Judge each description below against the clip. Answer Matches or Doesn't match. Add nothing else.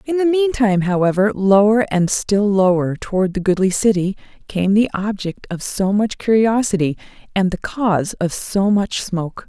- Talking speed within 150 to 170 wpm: Matches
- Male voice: Doesn't match